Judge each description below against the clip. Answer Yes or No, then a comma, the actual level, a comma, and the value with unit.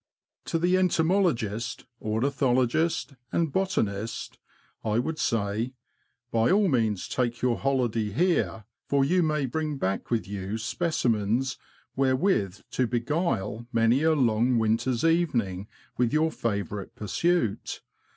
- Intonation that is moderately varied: No, wide, 6.1 semitones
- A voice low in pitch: Yes, low, 120 Hz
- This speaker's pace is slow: Yes, slow, 125 wpm